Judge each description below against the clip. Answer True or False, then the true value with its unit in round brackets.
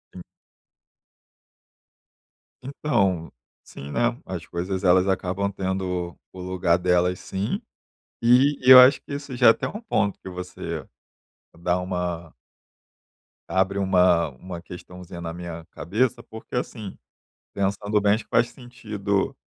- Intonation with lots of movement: False (3.5 semitones)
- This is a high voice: False (95 Hz)